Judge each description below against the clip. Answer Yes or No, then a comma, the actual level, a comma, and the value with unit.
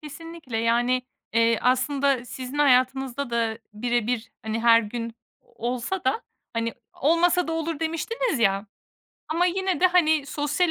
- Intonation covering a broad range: Yes, wide, 5.7 semitones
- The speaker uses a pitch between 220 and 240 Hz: No, very high, 260 Hz